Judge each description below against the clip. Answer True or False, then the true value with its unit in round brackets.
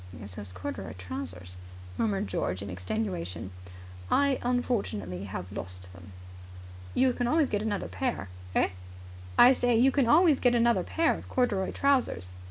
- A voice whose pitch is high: True (200 Hz)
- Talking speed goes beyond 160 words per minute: False (150 wpm)